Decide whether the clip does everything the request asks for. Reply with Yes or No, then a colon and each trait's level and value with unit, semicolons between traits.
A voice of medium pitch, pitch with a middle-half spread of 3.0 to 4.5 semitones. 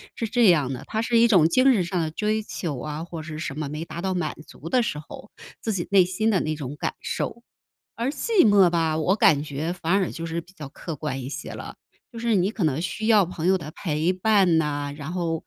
No: medium, 175 Hz; average, 4.9 semitones